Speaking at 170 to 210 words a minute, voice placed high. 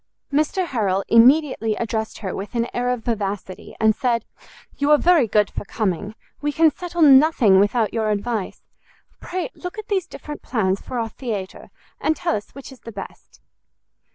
Yes: average, 175 wpm; high, 235 Hz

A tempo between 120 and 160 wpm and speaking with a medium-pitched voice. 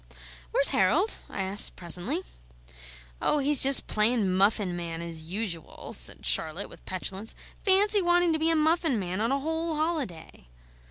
No: average, 155 wpm; high, 220 Hz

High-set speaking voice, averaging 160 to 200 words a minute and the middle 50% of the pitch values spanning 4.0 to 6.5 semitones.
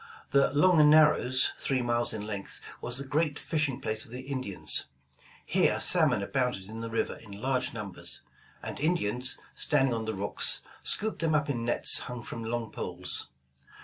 No: low, 125 Hz; average, 170 wpm; average, 4.3 semitones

